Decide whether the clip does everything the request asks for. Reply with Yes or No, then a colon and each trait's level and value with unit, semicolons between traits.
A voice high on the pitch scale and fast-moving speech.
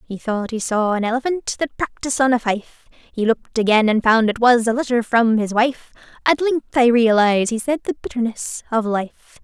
Yes: high, 235 Hz; fast, 210 wpm